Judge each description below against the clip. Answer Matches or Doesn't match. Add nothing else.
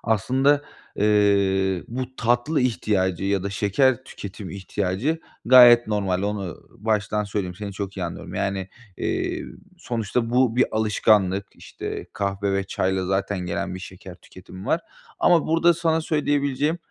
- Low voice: Matches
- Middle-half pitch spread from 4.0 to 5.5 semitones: Matches